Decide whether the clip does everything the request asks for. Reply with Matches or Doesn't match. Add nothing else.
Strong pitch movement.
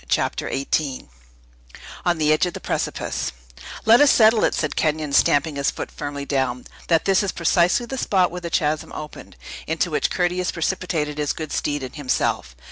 Doesn't match